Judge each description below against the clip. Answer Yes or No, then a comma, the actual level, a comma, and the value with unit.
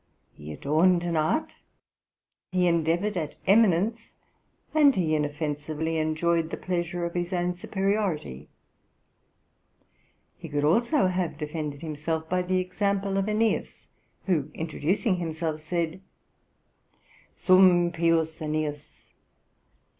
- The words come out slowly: Yes, slow, 110 wpm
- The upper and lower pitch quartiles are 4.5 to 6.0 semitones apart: No, average, 3.0 semitones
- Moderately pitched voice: Yes, medium, 170 Hz